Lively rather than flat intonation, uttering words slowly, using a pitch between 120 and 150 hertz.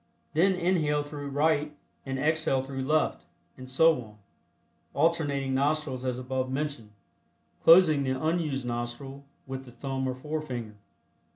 No: average, 2.9 semitones; slow, 130 wpm; medium, 140 Hz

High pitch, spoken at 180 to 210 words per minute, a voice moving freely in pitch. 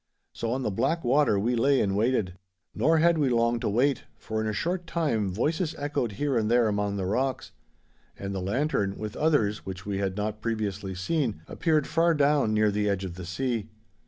No: low, 115 Hz; fast, 205 wpm; wide, 5.9 semitones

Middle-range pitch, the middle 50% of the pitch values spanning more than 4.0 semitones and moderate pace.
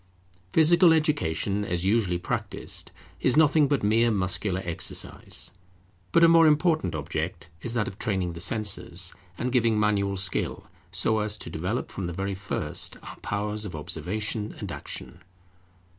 No: low, 105 Hz; average, 4.7 semitones; average, 150 wpm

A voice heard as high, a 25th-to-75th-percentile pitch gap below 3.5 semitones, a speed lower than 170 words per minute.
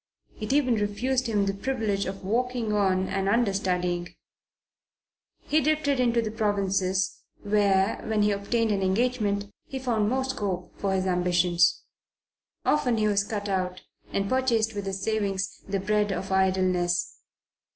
Yes: high, 205 Hz; average, 3.1 semitones; average, 140 wpm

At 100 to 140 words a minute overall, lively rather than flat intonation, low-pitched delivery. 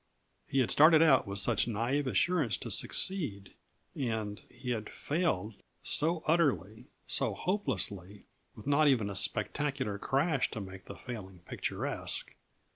Yes: slow, 135 wpm; wide, 6.5 semitones; low, 125 Hz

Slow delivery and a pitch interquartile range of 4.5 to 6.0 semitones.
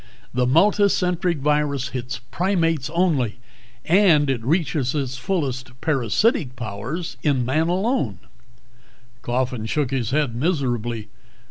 Yes: slow, 110 wpm; average, 5.2 semitones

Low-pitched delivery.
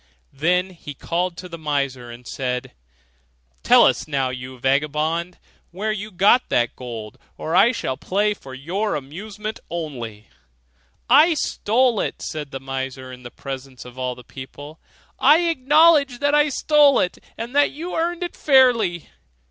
No: medium, 170 Hz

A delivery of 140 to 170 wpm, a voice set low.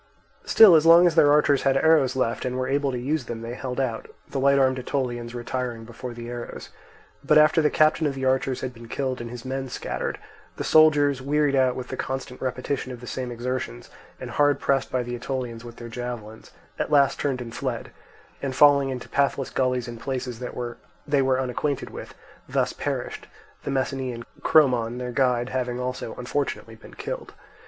No: average, 195 wpm; low, 130 Hz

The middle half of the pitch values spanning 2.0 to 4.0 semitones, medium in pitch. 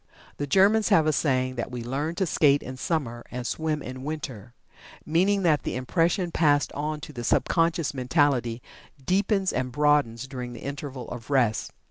No: average, 4.4 semitones; medium, 145 Hz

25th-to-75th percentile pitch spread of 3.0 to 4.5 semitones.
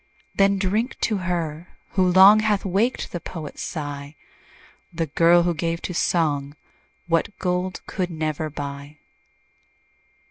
Yes: average, 3.5 semitones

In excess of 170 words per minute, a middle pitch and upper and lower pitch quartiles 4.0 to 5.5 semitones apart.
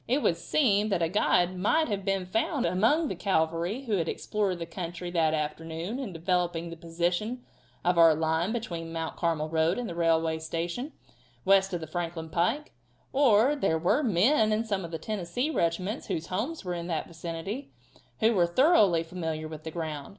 Yes: average, 190 wpm; medium, 175 Hz; average, 4.5 semitones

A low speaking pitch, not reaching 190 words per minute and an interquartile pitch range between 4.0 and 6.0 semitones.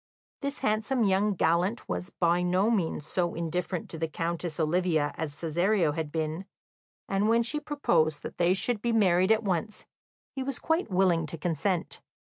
No: medium, 180 Hz; average, 170 wpm; average, 4.4 semitones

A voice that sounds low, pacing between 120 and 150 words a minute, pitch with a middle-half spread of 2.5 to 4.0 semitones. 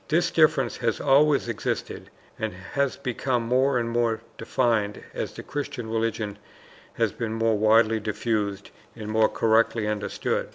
Yes: low, 115 Hz; average, 140 wpm; average, 2.9 semitones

